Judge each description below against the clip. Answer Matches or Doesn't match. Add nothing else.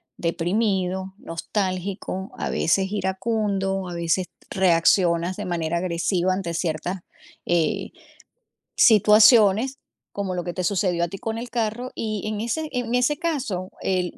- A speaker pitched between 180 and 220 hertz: Matches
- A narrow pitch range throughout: Doesn't match